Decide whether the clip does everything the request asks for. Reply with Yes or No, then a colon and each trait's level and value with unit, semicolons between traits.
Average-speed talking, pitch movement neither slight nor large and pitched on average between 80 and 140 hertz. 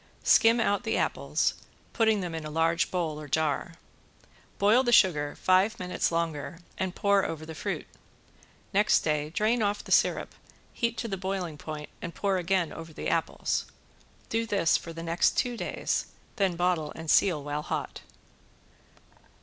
No: average, 165 wpm; average, 4.1 semitones; medium, 175 Hz